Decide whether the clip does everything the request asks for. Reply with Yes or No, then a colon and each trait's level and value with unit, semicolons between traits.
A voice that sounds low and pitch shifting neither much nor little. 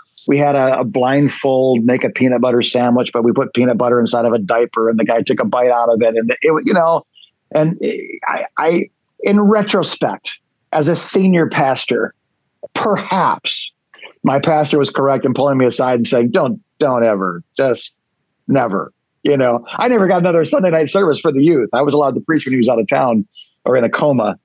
Yes: low, 130 Hz; average, 4.2 semitones